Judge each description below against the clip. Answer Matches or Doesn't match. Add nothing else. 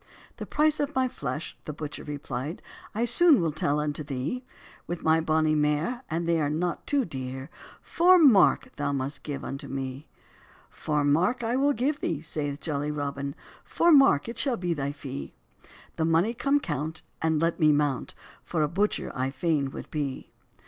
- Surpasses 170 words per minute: Matches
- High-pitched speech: Doesn't match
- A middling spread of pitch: Doesn't match